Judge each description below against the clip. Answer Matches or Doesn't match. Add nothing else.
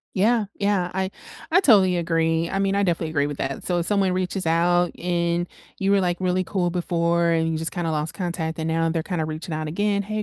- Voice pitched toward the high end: Doesn't match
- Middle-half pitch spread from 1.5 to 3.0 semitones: Matches